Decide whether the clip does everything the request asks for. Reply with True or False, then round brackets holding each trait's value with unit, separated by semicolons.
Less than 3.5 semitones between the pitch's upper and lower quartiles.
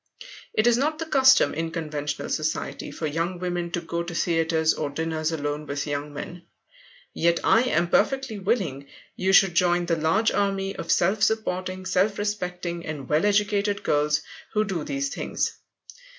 False (4.3 semitones)